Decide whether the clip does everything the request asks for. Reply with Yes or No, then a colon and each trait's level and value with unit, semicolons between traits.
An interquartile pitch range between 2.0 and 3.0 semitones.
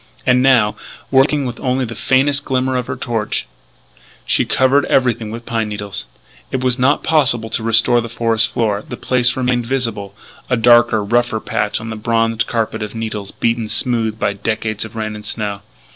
Yes: narrow, 2.6 semitones